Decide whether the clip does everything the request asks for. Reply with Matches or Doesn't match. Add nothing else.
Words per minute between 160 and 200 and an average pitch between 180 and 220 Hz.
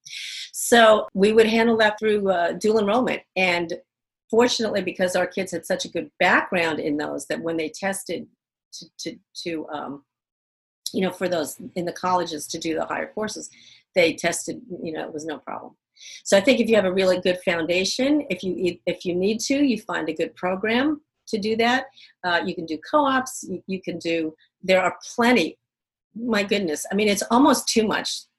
Matches